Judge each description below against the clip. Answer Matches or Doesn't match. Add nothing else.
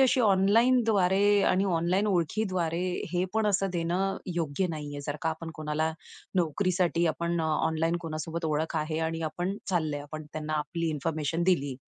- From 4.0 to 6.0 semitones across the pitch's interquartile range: Doesn't match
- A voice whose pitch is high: Doesn't match